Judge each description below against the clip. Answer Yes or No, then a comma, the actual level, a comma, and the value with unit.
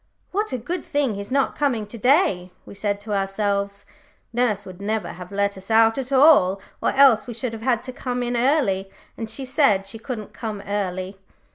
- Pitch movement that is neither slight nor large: Yes, average, 4.3 semitones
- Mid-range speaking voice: No, high, 220 Hz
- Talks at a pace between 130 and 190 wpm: No, fast, 205 wpm